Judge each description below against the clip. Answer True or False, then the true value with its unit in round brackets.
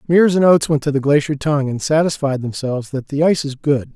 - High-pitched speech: False (145 Hz)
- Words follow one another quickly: True (245 wpm)